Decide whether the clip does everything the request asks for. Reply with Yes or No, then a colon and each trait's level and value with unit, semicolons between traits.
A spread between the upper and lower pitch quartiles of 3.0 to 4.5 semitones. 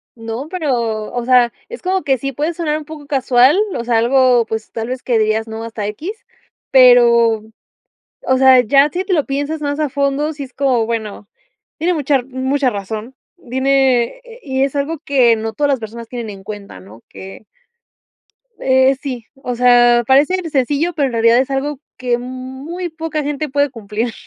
Yes: average, 3.6 semitones